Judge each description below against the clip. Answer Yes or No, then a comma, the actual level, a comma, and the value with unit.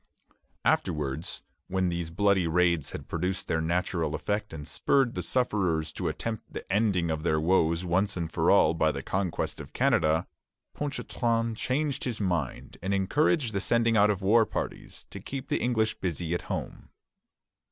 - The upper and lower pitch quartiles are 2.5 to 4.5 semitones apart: No, average, 5.2 semitones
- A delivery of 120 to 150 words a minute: No, average, 165 wpm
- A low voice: Yes, very low, 95 Hz